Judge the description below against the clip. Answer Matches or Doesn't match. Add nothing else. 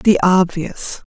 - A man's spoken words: Doesn't match